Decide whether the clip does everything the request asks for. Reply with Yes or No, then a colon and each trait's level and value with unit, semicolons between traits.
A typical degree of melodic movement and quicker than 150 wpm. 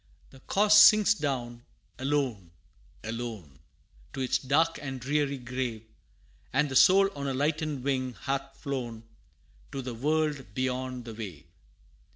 No: average, 3.4 semitones; slow, 135 wpm